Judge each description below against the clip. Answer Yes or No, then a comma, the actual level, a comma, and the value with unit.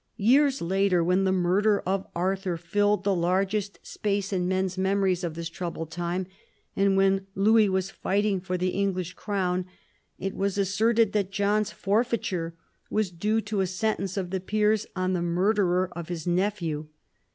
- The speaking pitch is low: No, high, 190 Hz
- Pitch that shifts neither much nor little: No, narrow, 2.2 semitones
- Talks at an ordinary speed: Yes, average, 165 wpm